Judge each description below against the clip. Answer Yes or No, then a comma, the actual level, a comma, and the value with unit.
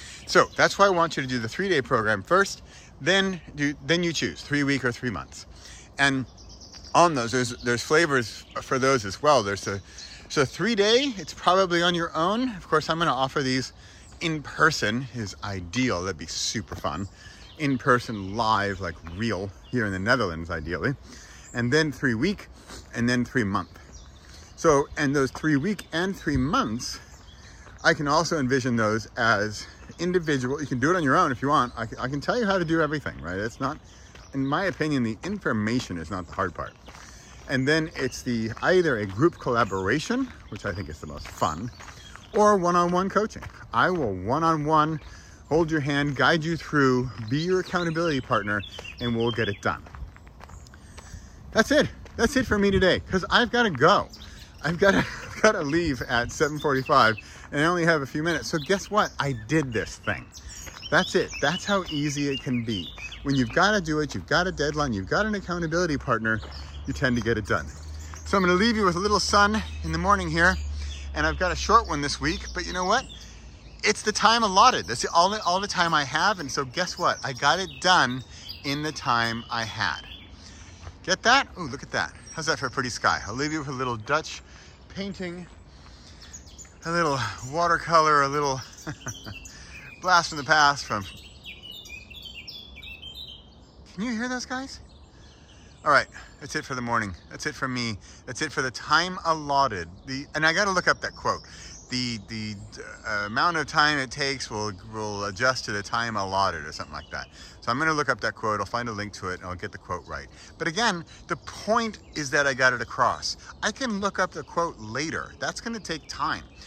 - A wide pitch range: Yes, wide, 8.7 semitones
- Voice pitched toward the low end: Yes, low, 130 Hz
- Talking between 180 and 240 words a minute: Yes, average, 200 wpm